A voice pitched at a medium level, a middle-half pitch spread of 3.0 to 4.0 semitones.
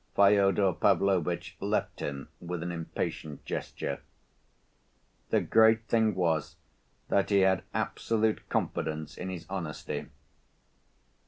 No: very low, 95 Hz; average, 3.4 semitones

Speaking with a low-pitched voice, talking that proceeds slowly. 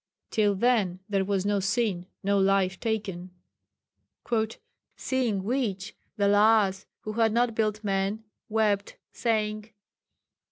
No: high, 205 Hz; slow, 115 wpm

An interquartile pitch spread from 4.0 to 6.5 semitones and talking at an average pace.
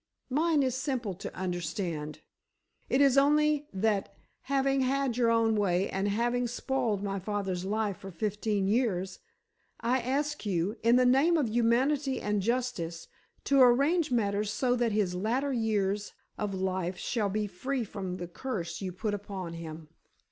Yes: average, 5.0 semitones; average, 155 wpm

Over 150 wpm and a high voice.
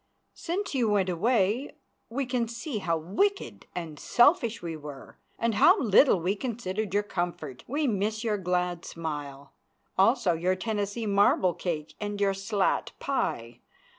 No: average, 145 wpm; high, 200 Hz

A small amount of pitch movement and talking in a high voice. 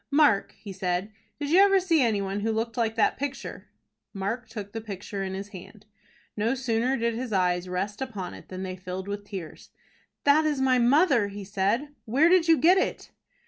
No: wide, 5.4 semitones; high, 220 Hz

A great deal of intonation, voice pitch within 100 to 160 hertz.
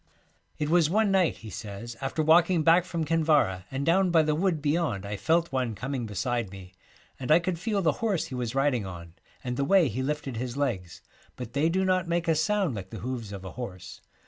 Yes: wide, 6.6 semitones; medium, 140 Hz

